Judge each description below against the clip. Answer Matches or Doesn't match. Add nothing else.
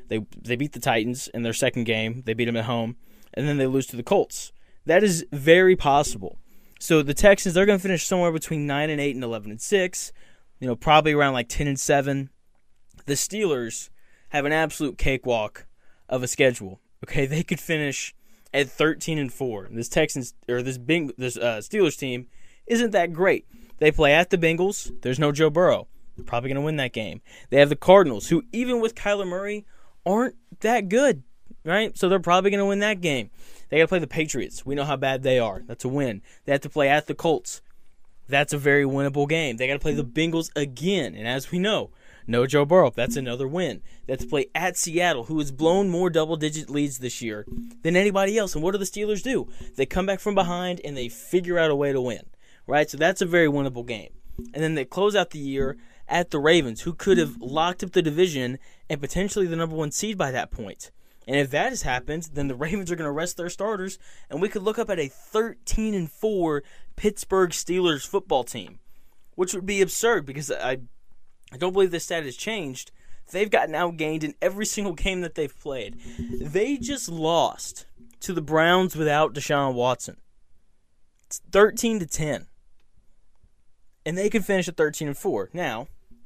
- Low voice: Doesn't match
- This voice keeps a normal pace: Doesn't match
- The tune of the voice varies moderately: Doesn't match